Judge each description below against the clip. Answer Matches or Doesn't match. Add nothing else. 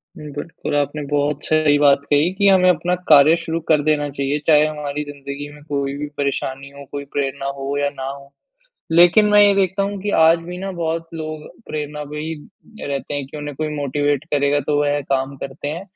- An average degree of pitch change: Doesn't match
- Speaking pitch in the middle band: Matches